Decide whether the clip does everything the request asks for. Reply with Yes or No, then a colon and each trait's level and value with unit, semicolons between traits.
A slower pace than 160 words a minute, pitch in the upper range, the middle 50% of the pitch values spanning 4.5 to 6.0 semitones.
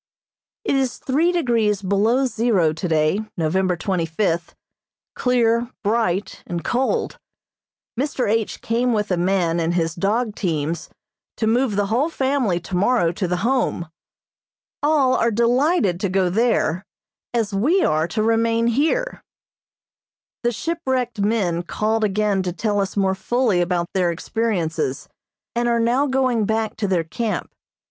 Yes: average, 140 wpm; high, 215 Hz; average, 5.1 semitones